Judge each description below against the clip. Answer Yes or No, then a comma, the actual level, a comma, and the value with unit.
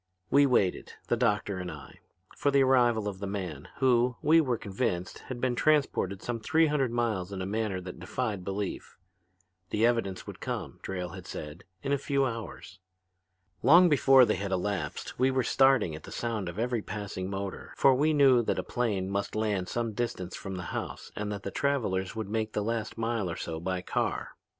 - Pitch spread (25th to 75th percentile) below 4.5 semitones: No, average, 4.9 semitones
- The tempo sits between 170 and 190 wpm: No, average, 200 wpm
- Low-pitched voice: Yes, low, 110 Hz